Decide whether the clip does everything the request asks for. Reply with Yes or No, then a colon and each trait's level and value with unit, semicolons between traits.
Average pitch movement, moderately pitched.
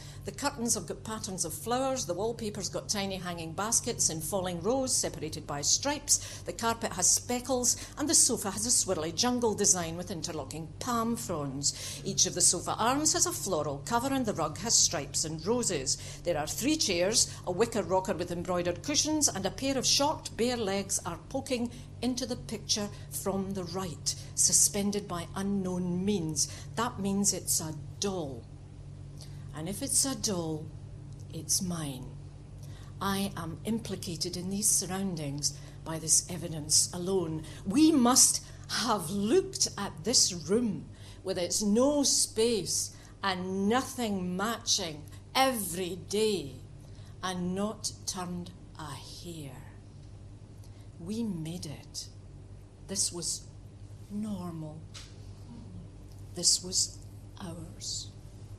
No: wide, 7.5 semitones; medium, 175 Hz